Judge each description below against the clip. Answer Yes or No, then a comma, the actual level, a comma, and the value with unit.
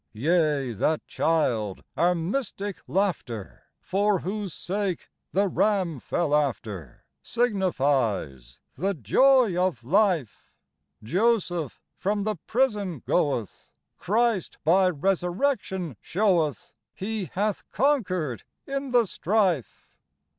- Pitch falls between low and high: Yes, medium, 180 Hz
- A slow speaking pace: Yes, slow, 95 wpm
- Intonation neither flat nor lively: No, wide, 6.0 semitones